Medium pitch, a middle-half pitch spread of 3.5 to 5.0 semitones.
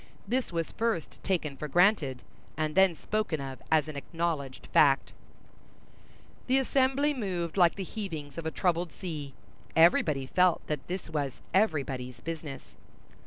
Yes: medium, 165 Hz; average, 4.7 semitones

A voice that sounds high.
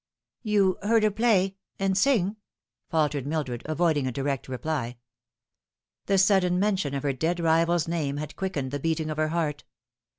No: medium, 165 Hz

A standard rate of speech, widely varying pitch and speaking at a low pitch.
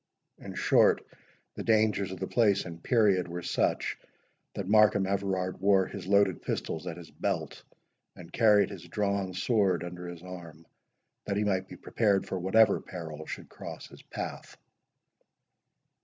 No: average, 155 wpm; narrow, 2.5 semitones; very low, 95 Hz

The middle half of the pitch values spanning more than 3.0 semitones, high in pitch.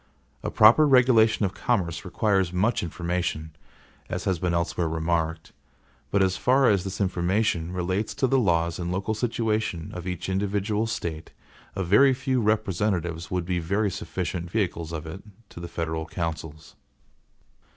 No: average, 4.1 semitones; very low, 90 Hz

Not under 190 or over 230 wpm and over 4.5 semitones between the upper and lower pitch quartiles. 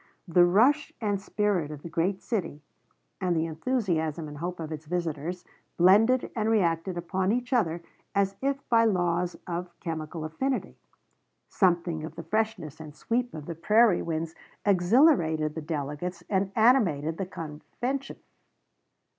No: average, 145 wpm; average, 5.0 semitones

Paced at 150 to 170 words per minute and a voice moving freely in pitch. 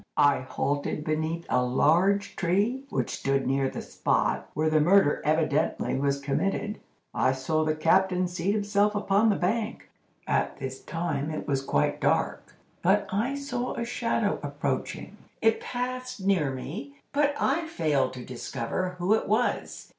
Yes: average, 155 wpm; wide, 6.5 semitones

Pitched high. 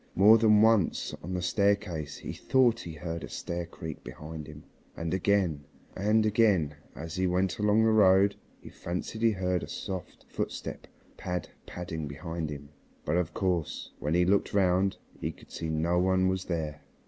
No: very low, 90 Hz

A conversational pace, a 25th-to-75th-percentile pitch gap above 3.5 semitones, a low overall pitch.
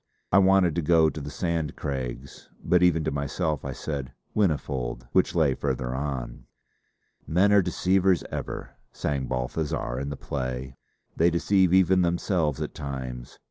Yes: average, 150 wpm; average, 5.2 semitones; very low, 75 Hz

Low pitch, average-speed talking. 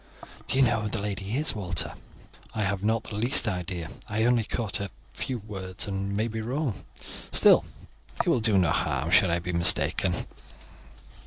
Yes: low, 105 Hz; average, 180 wpm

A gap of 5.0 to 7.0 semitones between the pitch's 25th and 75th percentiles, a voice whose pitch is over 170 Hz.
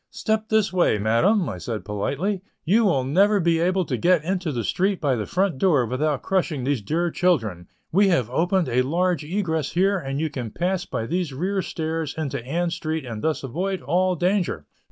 No: wide, 5.6 semitones; medium, 165 Hz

